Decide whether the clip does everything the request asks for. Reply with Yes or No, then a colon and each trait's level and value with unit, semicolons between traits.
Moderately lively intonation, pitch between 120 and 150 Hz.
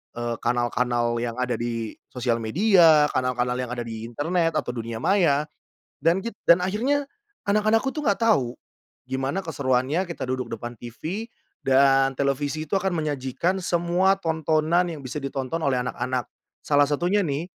No: wide, 6.0 semitones; medium, 140 Hz